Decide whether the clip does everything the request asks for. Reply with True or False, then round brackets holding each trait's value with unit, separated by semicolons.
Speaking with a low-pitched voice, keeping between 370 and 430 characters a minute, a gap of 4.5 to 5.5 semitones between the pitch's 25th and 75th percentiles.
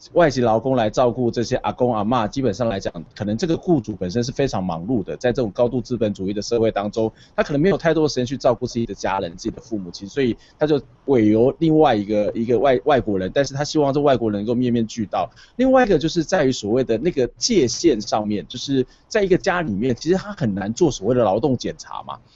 True (125 Hz; 375 characters per minute; 5.1 semitones)